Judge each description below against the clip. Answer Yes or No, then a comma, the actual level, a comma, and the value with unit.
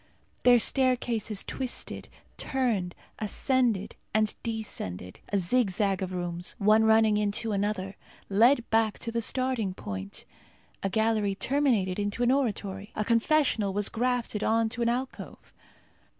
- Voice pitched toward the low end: No, high, 220 Hz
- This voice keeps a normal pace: No, slow, 130 wpm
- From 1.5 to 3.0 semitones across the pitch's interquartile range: No, average, 3.4 semitones